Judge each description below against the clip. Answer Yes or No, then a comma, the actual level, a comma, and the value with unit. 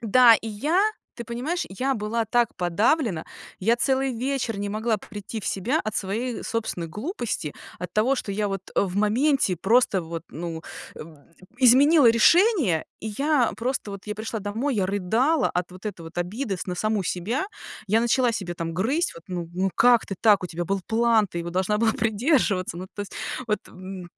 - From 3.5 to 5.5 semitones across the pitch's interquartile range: Yes, average, 4.7 semitones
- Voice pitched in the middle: No, high, 215 Hz